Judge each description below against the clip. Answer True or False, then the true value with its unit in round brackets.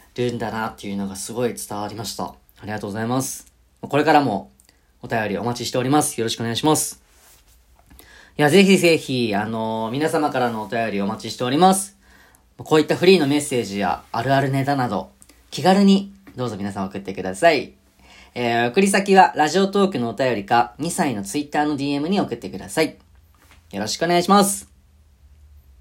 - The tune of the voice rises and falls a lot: True (7.0 semitones)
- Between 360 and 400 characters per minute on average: True (390 characters per minute)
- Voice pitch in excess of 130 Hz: False (120 Hz)